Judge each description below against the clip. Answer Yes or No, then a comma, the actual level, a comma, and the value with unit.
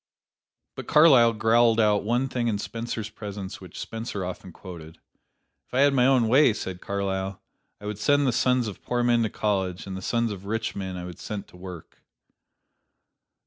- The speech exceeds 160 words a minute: Yes, average, 185 wpm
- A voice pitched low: Yes, low, 110 Hz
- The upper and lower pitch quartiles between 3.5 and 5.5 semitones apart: Yes, average, 3.8 semitones